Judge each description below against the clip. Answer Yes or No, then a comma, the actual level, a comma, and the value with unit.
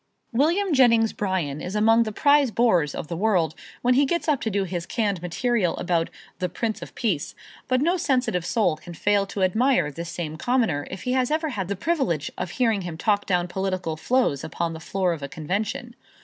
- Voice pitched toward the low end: No, high, 200 Hz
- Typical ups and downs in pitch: No, wide, 6.1 semitones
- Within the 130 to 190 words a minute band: No, fast, 205 wpm